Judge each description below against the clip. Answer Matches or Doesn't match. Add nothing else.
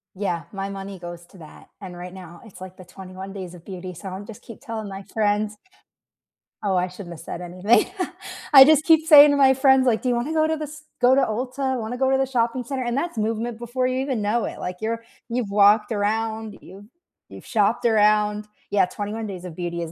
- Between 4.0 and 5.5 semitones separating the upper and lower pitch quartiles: Matches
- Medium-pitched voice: Doesn't match